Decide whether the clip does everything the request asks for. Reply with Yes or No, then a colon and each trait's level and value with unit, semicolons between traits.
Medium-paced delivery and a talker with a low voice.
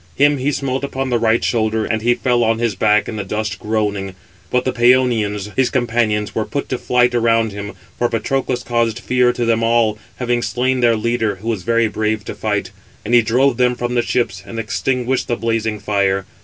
No: fast, 210 wpm; low, 115 Hz